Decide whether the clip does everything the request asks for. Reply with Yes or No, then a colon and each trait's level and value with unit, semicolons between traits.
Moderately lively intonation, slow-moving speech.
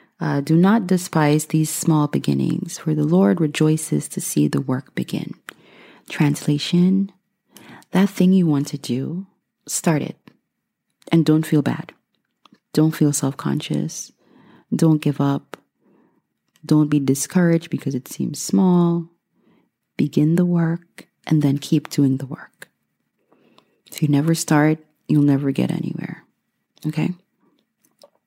Yes: average, 3.0 semitones; slow, 130 wpm